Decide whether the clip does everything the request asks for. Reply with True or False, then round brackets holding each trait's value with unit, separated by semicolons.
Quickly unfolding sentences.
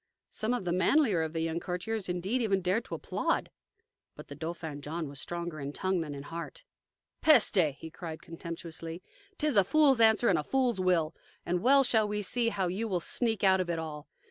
True (215 wpm)